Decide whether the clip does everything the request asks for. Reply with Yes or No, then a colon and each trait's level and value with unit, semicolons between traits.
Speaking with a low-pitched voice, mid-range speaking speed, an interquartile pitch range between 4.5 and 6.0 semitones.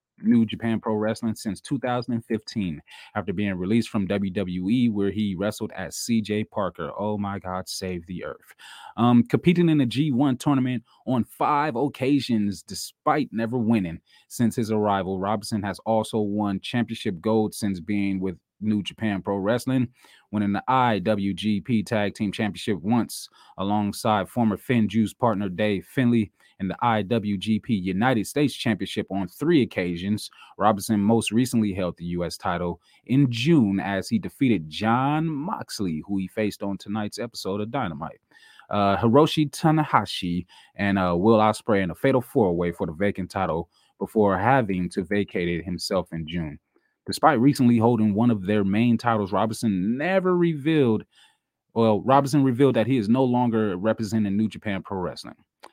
No: low, 110 Hz; average, 155 wpm; average, 3.3 semitones